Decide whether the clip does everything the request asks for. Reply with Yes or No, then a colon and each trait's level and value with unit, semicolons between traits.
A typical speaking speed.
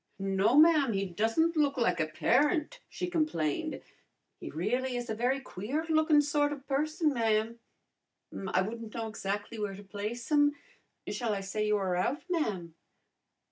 Yes: average, 160 wpm